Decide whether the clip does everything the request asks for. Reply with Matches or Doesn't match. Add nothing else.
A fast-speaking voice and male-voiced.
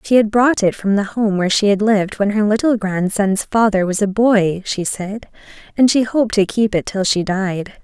Doesn't match